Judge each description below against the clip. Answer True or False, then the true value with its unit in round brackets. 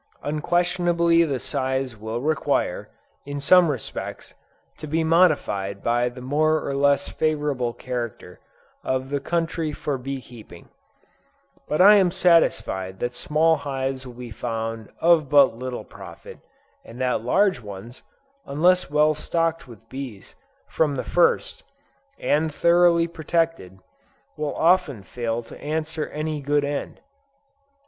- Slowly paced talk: True (130 wpm)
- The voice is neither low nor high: True (145 Hz)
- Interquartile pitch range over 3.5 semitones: True (4.9 semitones)